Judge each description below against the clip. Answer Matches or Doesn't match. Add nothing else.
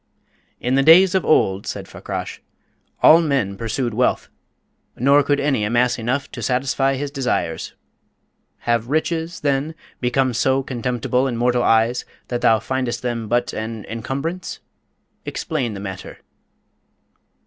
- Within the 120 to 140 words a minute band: Matches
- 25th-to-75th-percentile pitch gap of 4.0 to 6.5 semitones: Doesn't match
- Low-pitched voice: Matches